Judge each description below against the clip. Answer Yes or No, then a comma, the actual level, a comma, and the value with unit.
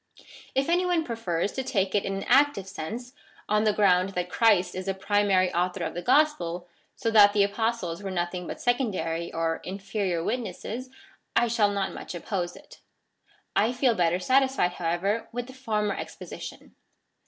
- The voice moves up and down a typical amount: Yes, average, 4.7 semitones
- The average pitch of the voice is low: No, high, 200 Hz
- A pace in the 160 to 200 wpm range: Yes, average, 170 wpm